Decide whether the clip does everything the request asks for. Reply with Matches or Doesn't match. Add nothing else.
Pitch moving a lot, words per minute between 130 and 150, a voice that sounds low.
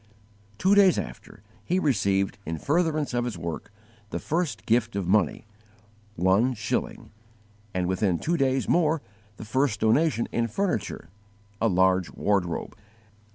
Matches